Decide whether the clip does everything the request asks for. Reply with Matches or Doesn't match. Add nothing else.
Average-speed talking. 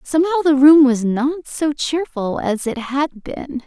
Matches